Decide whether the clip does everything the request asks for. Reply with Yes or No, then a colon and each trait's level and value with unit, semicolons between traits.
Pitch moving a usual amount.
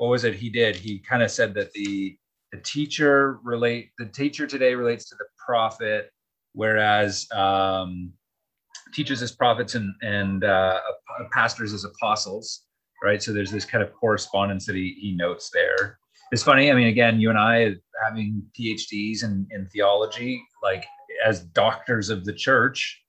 Yes: average, 3.1 semitones